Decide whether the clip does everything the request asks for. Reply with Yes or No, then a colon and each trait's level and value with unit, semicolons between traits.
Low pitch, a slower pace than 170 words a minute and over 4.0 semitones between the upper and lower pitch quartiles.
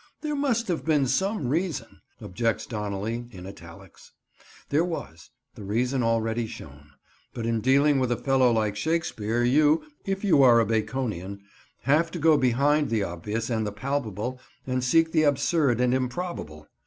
Yes: low, 125 Hz; average, 155 wpm; wide, 5.6 semitones